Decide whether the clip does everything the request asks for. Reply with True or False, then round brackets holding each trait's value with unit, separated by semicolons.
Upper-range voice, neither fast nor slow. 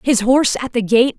False (245 Hz; 255 wpm)